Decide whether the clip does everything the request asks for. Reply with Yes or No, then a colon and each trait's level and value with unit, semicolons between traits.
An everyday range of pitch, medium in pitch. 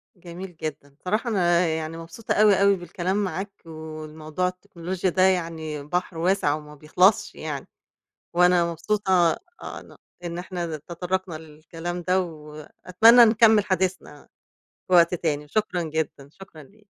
Yes: average, 3.0 semitones; medium, 175 Hz